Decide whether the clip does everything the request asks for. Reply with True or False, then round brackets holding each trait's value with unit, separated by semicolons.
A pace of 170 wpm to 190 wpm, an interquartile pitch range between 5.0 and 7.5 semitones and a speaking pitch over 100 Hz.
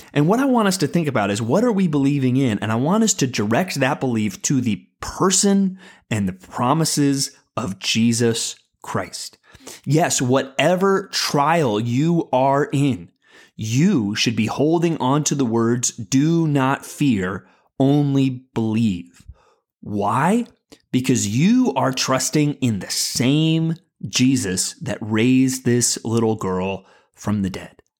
False (145 wpm; 5.5 semitones; 135 Hz)